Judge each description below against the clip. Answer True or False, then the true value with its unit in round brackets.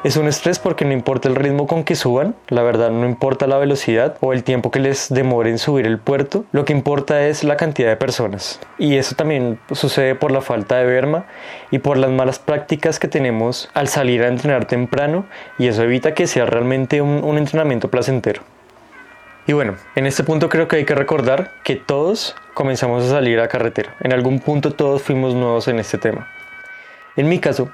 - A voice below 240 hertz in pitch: True (135 Hz)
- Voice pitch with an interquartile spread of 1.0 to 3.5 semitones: True (2.9 semitones)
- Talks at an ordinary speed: False (205 wpm)